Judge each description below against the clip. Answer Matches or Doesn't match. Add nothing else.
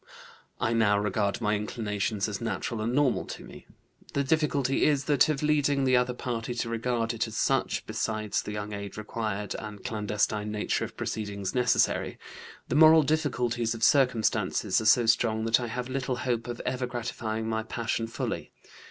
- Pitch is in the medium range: Doesn't match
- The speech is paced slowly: Doesn't match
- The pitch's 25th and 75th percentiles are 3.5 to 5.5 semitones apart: Doesn't match